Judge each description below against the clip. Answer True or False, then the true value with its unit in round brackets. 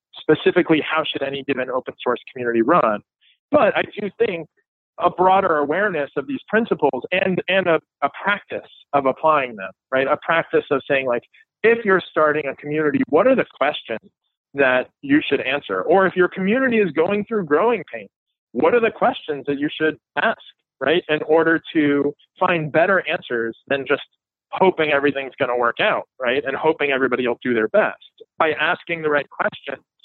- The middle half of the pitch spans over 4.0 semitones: True (5.4 semitones)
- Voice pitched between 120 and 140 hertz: False (155 Hz)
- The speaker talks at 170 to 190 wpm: True (180 wpm)